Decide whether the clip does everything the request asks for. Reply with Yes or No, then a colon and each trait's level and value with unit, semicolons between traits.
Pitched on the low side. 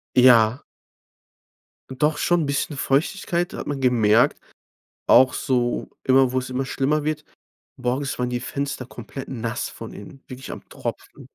Yes: low, 130 Hz